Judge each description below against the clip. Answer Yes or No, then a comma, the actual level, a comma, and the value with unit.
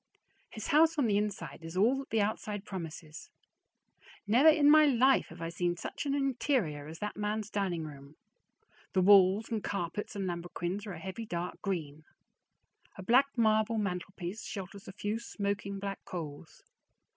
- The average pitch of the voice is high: Yes, high, 200 Hz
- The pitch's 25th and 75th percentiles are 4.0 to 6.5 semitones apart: Yes, average, 4.3 semitones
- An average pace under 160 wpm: No, average, 165 wpm